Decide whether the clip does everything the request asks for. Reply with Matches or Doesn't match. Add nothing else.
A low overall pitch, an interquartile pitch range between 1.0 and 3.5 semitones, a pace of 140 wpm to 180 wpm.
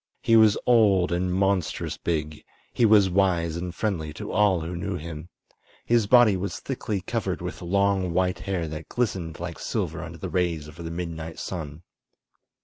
Matches